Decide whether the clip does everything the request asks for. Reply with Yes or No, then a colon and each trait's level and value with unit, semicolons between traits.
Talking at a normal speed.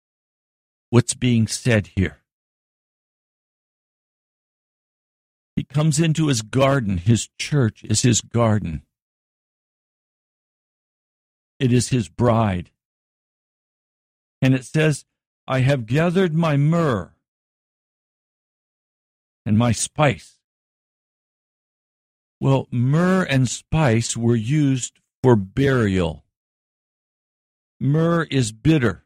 No: slow, 85 wpm